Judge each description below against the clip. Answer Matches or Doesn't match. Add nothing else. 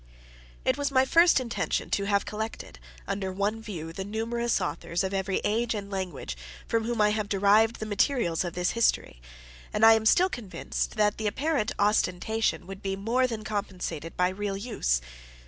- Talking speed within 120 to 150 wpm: Doesn't match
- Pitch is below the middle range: Doesn't match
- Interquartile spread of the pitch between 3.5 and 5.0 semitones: Doesn't match